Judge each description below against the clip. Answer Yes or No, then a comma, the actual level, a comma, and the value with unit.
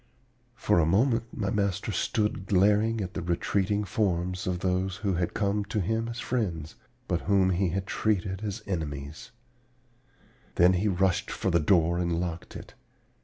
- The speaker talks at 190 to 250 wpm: No, average, 165 wpm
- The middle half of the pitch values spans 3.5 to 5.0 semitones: No, average, 3.0 semitones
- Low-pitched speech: Yes, very low, 95 Hz